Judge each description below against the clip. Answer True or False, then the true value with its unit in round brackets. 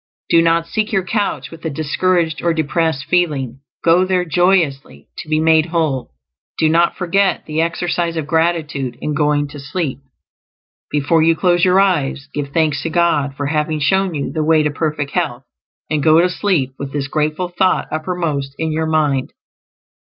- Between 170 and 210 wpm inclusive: True (175 wpm)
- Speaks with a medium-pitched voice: True (160 Hz)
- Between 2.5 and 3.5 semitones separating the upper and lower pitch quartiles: True (2.9 semitones)